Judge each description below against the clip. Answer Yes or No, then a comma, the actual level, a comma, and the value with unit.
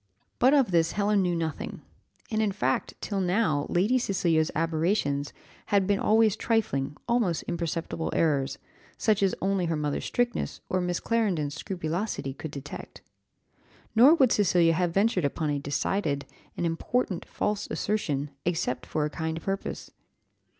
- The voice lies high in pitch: No, medium, 175 Hz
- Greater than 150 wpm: No, average, 145 wpm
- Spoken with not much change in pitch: No, average, 5.0 semitones